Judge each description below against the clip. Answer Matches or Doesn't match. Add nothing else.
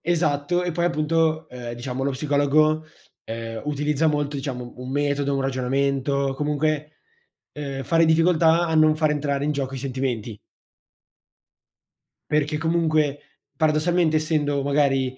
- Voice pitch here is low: Doesn't match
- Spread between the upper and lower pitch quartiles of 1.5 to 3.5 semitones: Matches